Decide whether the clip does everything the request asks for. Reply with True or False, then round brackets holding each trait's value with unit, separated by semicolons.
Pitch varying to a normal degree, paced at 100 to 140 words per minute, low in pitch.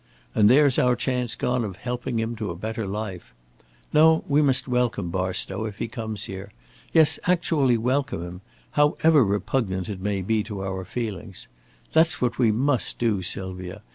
False (4.7 semitones; 170 wpm; 110 Hz)